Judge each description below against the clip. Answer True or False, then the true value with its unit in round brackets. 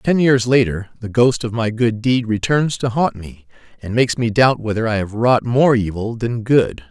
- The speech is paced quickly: True (215 wpm)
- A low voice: True (115 Hz)